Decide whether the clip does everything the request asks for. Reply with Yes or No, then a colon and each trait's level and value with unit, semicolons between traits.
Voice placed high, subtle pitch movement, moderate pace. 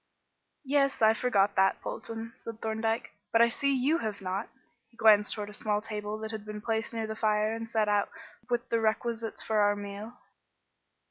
Yes: high, 220 Hz; narrow, 1.6 semitones; average, 190 wpm